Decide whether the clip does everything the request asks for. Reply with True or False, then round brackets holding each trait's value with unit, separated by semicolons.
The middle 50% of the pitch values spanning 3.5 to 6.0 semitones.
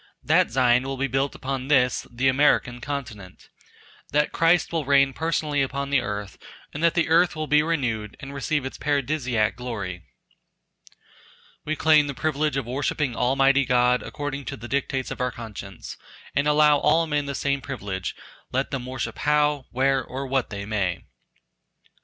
False (3.1 semitones)